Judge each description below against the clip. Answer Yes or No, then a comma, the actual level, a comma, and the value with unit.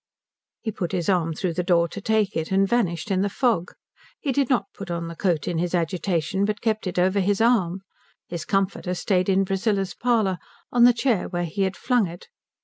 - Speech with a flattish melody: No, average, 3.4 semitones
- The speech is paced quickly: Yes, fast, 215 wpm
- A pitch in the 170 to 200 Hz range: Yes, high, 190 Hz